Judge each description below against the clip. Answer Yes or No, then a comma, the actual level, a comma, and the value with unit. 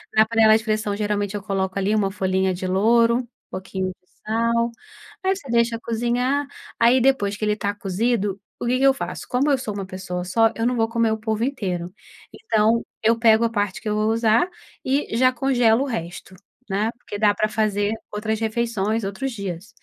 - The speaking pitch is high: Yes, high, 220 Hz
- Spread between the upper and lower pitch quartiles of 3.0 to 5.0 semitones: No, narrow, 2.6 semitones